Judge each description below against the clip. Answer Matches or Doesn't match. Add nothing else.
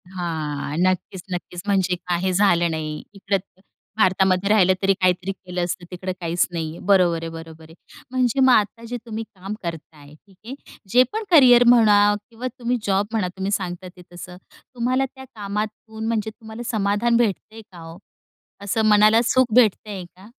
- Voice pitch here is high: Matches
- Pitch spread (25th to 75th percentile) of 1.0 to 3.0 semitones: Doesn't match